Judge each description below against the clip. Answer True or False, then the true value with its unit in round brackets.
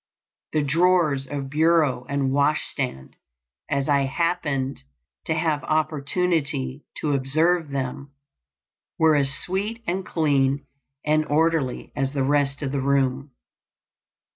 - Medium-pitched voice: True (145 Hz)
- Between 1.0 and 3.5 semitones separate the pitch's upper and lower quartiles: True (2.7 semitones)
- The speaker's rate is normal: False (120 wpm)